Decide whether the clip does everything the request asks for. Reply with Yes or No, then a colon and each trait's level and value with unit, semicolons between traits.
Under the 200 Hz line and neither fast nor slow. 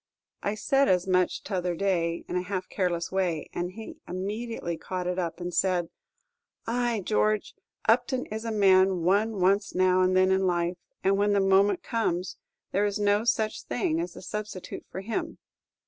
Yes: high, 190 Hz; average, 180 wpm